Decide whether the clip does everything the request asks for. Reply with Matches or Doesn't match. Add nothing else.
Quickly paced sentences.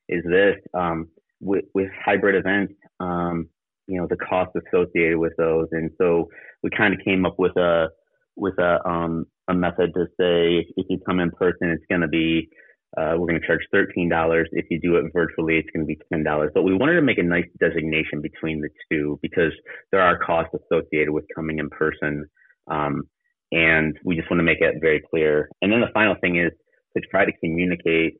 Matches